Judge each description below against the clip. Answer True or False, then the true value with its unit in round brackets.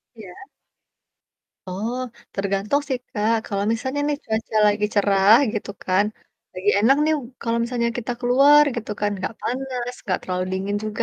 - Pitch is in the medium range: False (220 Hz)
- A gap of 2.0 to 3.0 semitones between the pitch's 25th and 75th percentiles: False (3.7 semitones)